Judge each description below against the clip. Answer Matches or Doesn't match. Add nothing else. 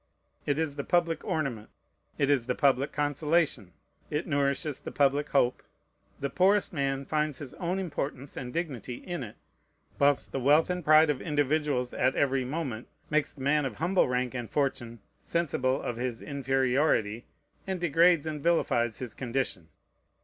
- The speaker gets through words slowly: Doesn't match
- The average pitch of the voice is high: Doesn't match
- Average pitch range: Matches